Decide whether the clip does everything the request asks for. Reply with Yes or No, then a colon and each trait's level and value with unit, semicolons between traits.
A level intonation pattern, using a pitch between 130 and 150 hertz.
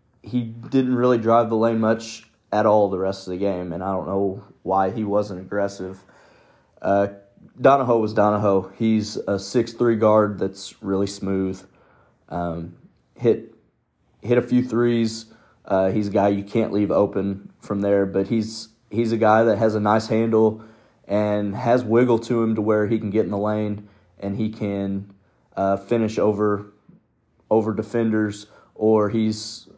No: narrow, 2.2 semitones; low, 105 Hz